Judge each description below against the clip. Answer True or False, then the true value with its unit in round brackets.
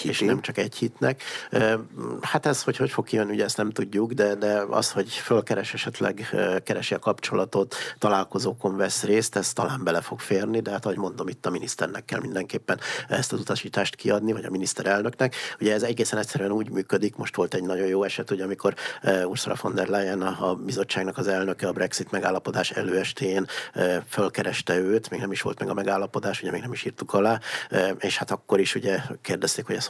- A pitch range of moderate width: False (2.3 semitones)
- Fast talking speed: True (195 wpm)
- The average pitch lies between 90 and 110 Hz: True (100 Hz)